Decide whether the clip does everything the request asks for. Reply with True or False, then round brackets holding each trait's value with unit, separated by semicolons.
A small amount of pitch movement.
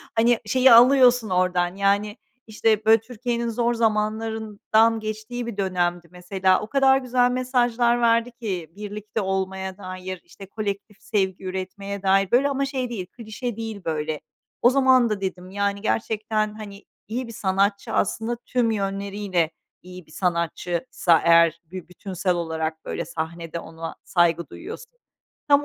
False (4.1 semitones)